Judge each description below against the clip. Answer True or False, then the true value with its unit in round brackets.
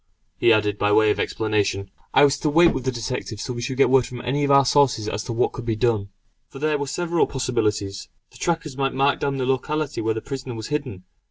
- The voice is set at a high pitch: False (125 Hz)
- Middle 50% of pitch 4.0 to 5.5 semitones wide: True (4.4 semitones)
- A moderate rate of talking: False (245 wpm)